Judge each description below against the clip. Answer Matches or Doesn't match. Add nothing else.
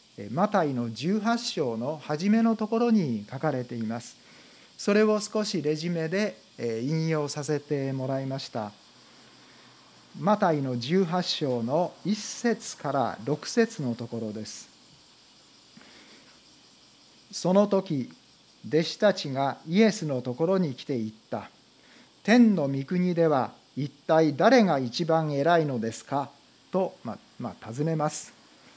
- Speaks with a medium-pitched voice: Matches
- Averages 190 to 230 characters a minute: Matches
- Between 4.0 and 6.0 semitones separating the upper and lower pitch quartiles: Doesn't match